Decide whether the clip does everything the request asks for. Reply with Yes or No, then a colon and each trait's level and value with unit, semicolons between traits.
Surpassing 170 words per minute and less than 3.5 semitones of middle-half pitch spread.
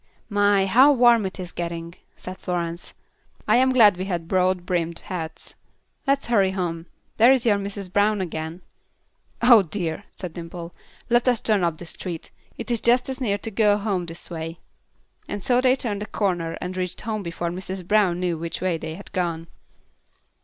No: average, 180 wpm; average, 3.9 semitones